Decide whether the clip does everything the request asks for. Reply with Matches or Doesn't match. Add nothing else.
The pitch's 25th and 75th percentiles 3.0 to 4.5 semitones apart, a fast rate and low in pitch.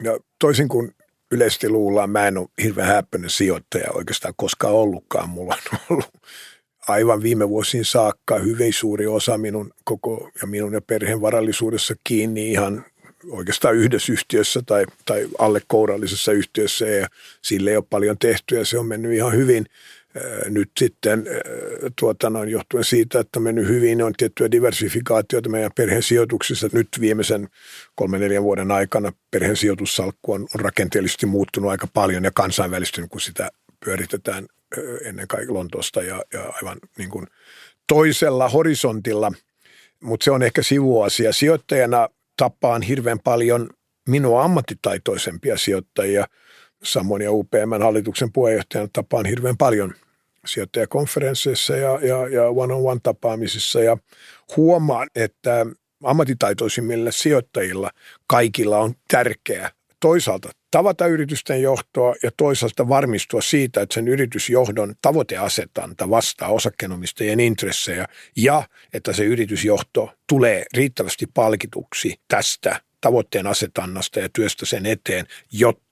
Doesn't match